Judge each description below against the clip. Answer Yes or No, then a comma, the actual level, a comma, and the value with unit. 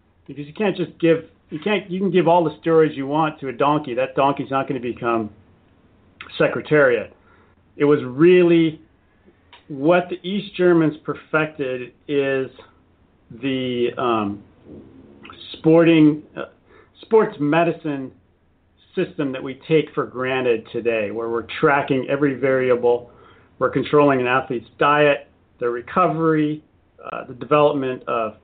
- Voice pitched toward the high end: No, medium, 140 Hz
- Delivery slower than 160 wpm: Yes, slow, 135 wpm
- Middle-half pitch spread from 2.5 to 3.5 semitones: No, average, 5.1 semitones